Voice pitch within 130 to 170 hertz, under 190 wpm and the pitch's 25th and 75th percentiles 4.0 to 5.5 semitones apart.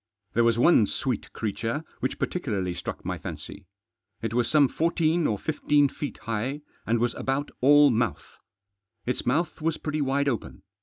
Yes: low, 135 Hz; average, 165 wpm; average, 4.5 semitones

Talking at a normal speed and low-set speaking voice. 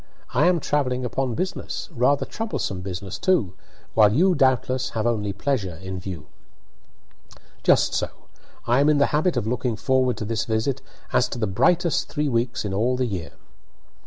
Yes: average, 170 wpm; low, 125 Hz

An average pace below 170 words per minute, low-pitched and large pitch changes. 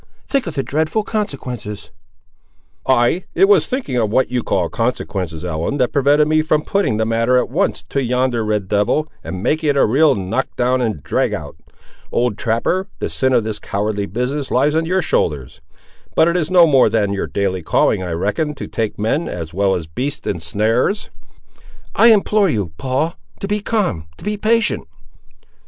No: average, 185 wpm; low, 125 Hz; wide, 7.3 semitones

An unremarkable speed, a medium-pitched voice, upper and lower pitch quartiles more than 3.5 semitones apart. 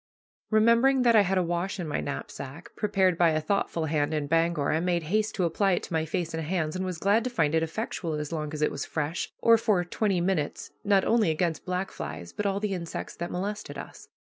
No: fast, 235 wpm; medium, 175 Hz; average, 4.1 semitones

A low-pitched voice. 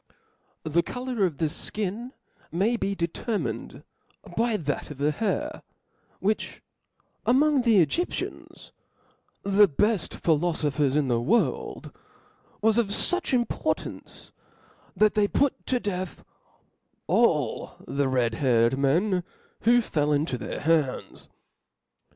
No: medium, 185 Hz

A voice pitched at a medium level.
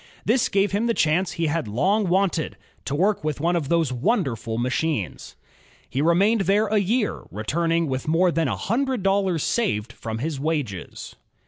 Yes: medium, 165 Hz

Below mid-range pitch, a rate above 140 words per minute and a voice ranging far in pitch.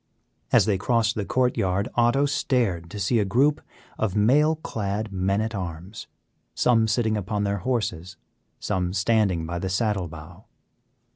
No: low, 105 Hz; average, 155 wpm; average, 3.8 semitones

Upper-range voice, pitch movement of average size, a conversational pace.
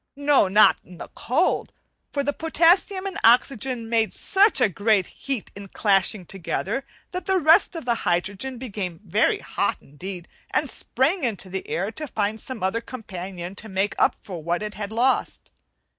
No: high, 220 Hz; wide, 5.9 semitones; average, 175 wpm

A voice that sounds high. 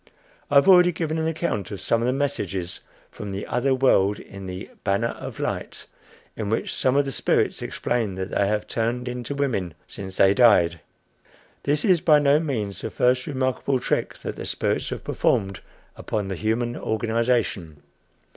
No: low, 115 Hz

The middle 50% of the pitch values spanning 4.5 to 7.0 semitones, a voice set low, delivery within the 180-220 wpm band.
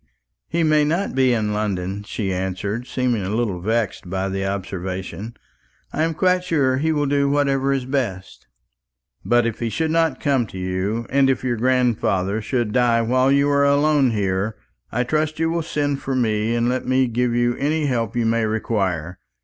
Yes: average, 5.1 semitones; low, 120 Hz; average, 190 wpm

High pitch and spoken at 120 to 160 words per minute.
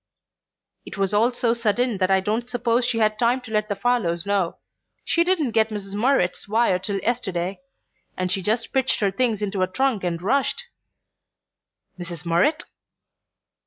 No: high, 215 Hz; average, 170 wpm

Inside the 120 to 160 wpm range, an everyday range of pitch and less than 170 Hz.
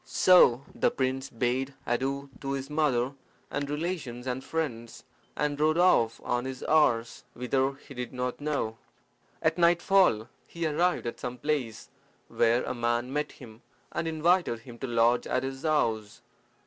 Yes: average, 155 wpm; average, 4.0 semitones; low, 135 Hz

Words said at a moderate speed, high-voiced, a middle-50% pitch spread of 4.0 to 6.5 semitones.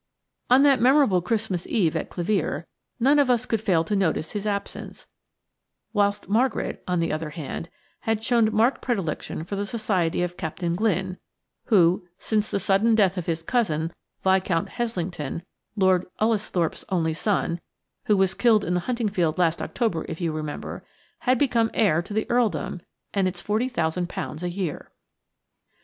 Yes: average, 160 wpm; high, 195 Hz; average, 4.4 semitones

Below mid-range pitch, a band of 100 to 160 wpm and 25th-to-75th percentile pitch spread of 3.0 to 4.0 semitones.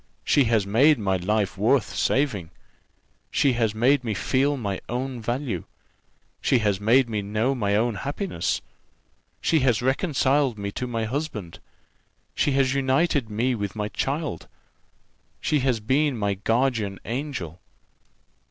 No: low, 120 Hz; average, 140 wpm; average, 4.6 semitones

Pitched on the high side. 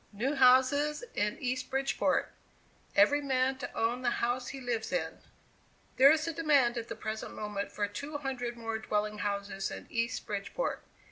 Yes: high, 245 Hz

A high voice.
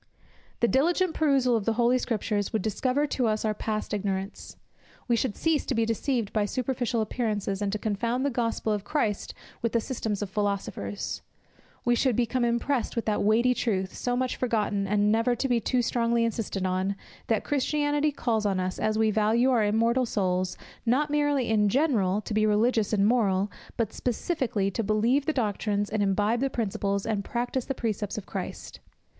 Yes: high, 225 Hz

